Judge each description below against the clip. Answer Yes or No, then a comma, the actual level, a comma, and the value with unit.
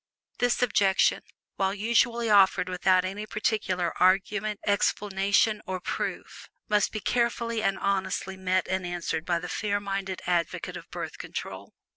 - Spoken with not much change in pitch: Yes, narrow, 2.2 semitones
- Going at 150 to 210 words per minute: No, average, 140 wpm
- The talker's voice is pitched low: No, high, 195 Hz